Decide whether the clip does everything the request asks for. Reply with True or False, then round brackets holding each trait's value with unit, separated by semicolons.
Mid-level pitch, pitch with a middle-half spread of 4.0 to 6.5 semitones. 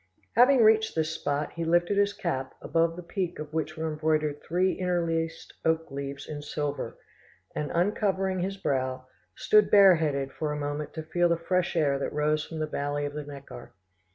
False (160 Hz; 3.5 semitones)